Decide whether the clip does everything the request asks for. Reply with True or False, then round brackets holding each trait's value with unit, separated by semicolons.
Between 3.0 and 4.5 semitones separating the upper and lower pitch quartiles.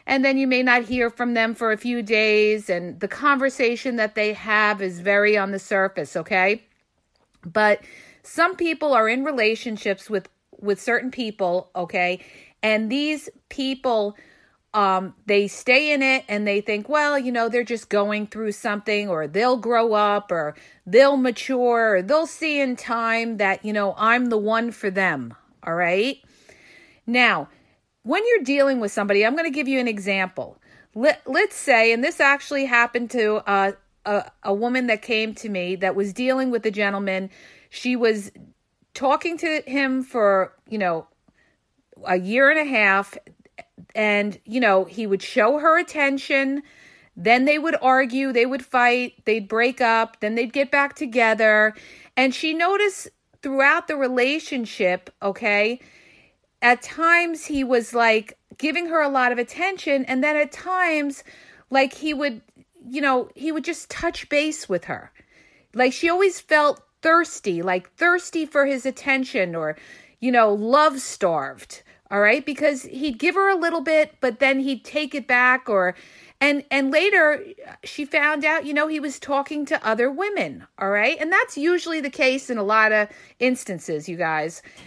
False (5.6 semitones)